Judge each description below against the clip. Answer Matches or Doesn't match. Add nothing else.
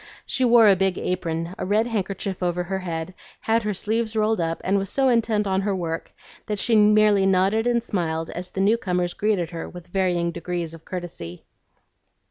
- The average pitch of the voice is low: Doesn't match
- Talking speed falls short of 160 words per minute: Doesn't match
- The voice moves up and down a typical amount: Matches